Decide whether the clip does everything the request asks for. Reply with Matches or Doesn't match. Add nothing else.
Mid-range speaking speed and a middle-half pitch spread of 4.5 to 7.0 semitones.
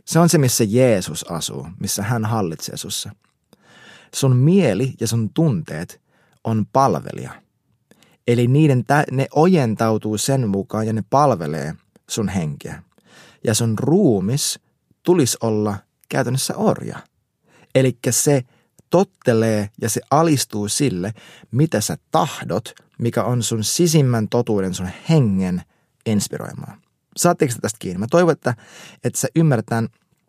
Matches